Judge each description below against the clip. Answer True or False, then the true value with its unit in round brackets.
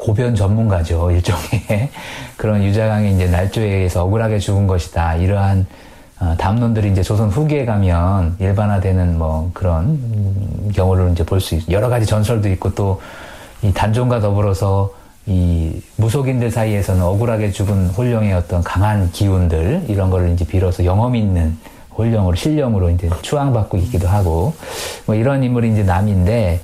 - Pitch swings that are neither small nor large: True (3.3 semitones)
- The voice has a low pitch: True (100 Hz)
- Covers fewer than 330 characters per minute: False (340 characters per minute)